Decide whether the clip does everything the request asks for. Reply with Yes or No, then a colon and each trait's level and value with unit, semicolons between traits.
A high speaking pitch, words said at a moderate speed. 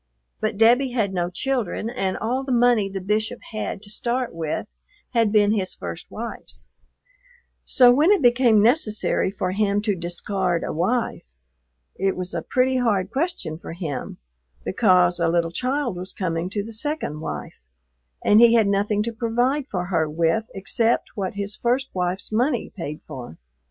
Yes: high, 210 Hz; average, 165 wpm